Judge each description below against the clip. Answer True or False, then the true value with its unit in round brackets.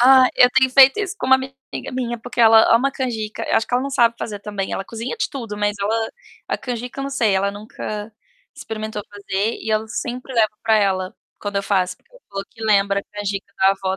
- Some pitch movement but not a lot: True (3.6 semitones)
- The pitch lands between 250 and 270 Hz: False (220 Hz)